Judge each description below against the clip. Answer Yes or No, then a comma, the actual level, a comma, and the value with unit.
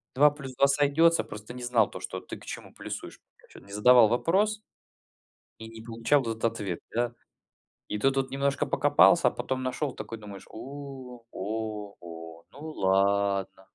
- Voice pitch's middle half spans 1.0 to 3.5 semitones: No, average, 4.9 semitones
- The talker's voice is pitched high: No, low, 120 Hz